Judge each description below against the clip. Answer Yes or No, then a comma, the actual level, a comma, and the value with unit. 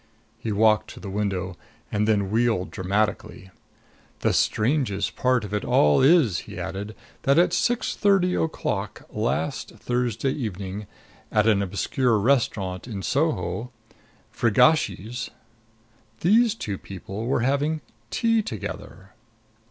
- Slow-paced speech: Yes, slow, 120 wpm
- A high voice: No, low, 110 Hz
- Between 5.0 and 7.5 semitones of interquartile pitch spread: Yes, average, 5.3 semitones